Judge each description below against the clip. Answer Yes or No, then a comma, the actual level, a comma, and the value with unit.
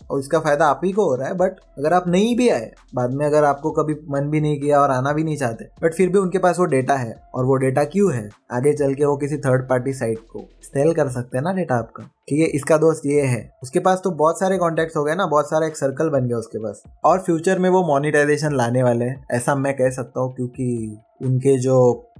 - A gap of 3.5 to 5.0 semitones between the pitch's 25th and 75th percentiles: Yes, average, 4.0 semitones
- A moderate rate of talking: No, fast, 260 wpm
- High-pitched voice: No, medium, 145 Hz